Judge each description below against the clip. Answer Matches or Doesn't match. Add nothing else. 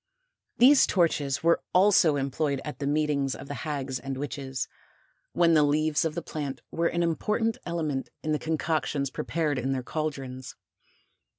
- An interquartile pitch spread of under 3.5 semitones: Matches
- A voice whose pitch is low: Doesn't match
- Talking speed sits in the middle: Matches